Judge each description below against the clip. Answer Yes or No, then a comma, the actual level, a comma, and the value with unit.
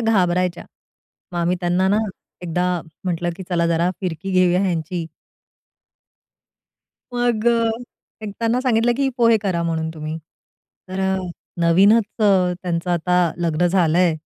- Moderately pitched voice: Yes, medium, 180 Hz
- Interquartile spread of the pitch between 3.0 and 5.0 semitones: No, narrow, 2.6 semitones